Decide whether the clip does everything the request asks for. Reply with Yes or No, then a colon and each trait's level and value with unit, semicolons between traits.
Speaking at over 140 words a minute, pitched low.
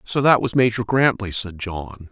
Yes: average, 200 wpm; low, 110 Hz